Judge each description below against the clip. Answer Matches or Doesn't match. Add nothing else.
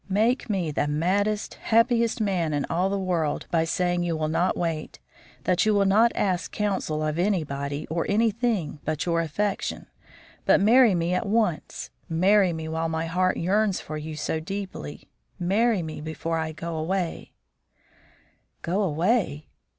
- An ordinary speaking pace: Matches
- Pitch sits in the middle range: Matches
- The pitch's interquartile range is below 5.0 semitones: Matches